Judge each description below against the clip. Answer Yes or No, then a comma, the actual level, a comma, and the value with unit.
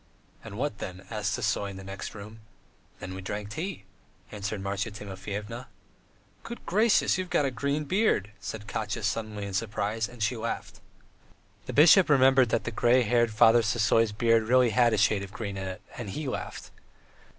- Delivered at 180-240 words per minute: Yes, average, 185 wpm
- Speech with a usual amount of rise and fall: Yes, average, 3.6 semitones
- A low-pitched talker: Yes, low, 110 Hz